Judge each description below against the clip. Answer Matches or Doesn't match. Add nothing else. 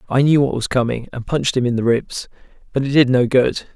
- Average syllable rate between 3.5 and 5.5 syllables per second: Doesn't match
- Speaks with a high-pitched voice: Doesn't match